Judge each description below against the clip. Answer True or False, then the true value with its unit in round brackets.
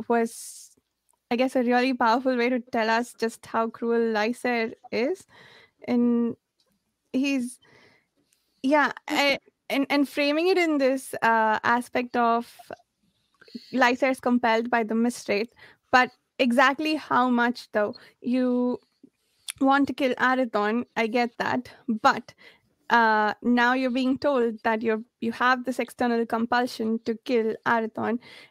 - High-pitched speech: True (245 Hz)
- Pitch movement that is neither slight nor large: False (2.2 semitones)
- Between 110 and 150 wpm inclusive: True (135 wpm)